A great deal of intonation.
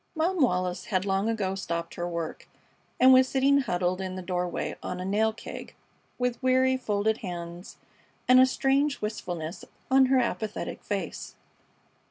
Yes: wide, 6.2 semitones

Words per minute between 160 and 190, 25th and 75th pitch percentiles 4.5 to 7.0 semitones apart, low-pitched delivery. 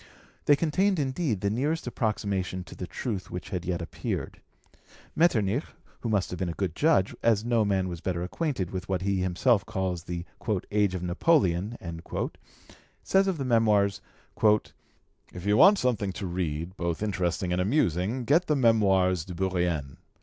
Yes: average, 165 wpm; average, 4.9 semitones; low, 100 Hz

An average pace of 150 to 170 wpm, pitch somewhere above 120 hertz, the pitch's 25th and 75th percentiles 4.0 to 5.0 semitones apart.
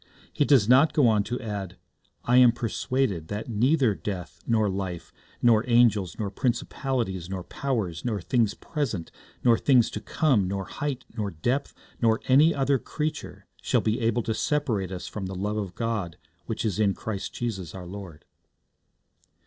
No: average, 165 wpm; low, 110 Hz; average, 4.5 semitones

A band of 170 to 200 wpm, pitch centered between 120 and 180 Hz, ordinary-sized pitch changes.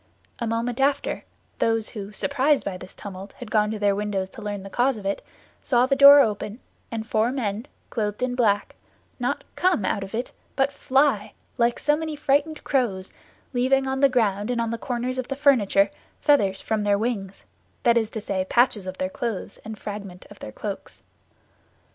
No: average, 190 wpm; high, 225 Hz; average, 4.4 semitones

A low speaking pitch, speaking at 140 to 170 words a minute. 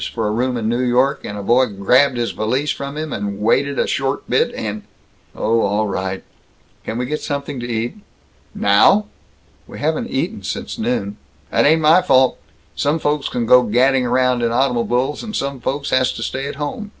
No: low, 125 Hz; average, 200 wpm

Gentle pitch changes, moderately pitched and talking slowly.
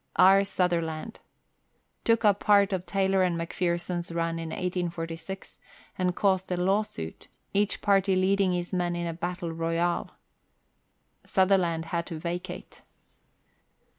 Yes: narrow, 2.3 semitones; medium, 180 Hz; slow, 130 wpm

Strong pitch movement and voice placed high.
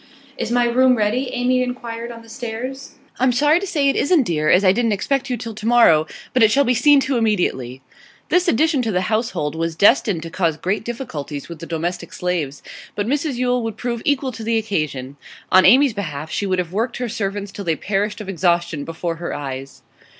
Yes: wide, 6.4 semitones; high, 220 Hz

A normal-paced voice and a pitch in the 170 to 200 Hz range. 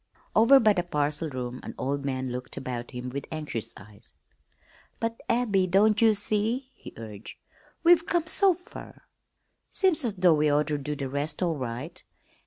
No: average, 170 wpm; medium, 155 Hz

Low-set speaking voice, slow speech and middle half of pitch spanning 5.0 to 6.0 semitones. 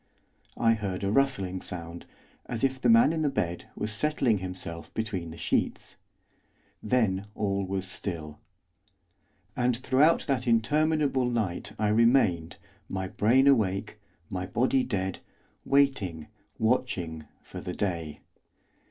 Yes: low, 105 Hz; slow, 125 wpm; wide, 5.6 semitones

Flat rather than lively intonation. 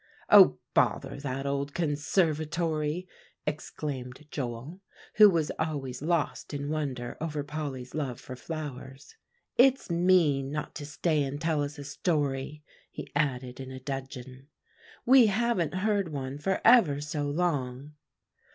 No: average, 3.4 semitones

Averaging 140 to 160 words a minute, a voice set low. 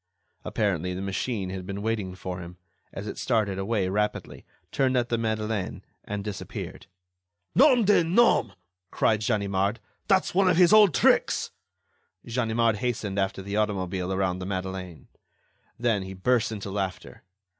Yes: average, 145 wpm; low, 105 Hz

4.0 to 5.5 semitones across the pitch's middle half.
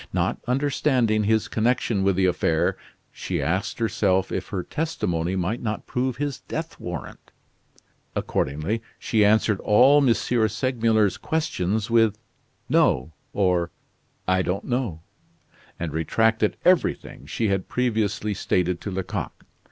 Yes: average, 4.5 semitones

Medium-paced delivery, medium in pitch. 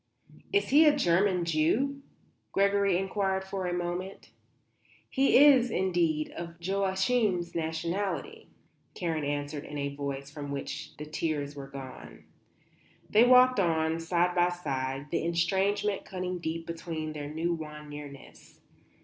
No: slow, 130 wpm; medium, 170 Hz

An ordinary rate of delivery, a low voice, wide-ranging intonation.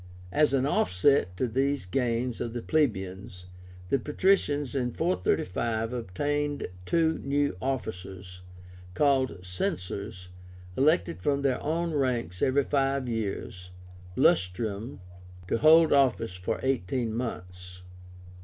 No: slow, 110 wpm; low, 120 Hz; wide, 7.4 semitones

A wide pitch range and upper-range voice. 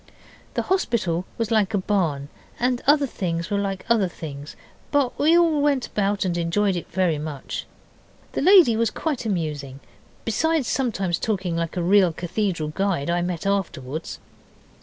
Yes: wide, 5.7 semitones; high, 195 Hz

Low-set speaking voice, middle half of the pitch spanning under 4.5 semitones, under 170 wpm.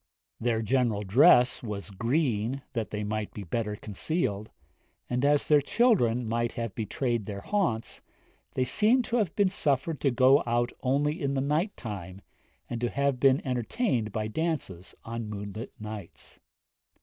No: low, 120 Hz; average, 4.8 semitones; average, 160 wpm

